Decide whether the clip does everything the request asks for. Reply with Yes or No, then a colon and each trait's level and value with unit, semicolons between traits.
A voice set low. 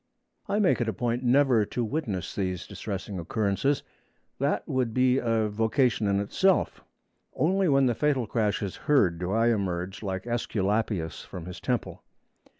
Yes: low, 115 Hz